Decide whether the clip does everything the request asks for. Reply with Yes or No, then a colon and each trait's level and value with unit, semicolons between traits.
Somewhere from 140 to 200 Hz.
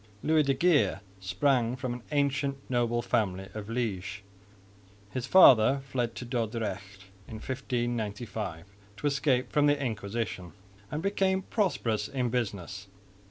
No: low, 120 Hz